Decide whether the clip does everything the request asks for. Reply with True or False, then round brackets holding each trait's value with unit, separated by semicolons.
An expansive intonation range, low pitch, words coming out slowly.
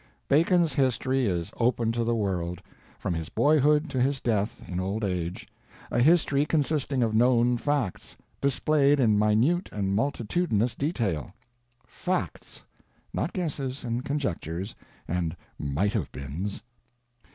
True (6.4 semitones; 120 Hz; 125 wpm)